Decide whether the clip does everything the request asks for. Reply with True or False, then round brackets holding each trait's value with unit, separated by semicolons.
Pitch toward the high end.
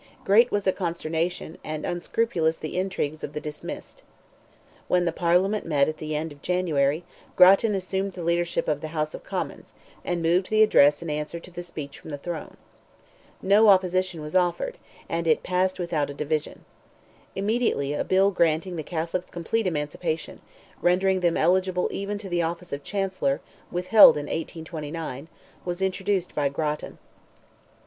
False (175 Hz)